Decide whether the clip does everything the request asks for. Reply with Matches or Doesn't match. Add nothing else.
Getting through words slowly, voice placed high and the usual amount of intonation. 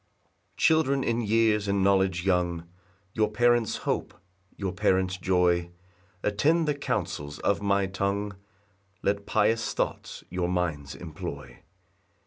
Doesn't match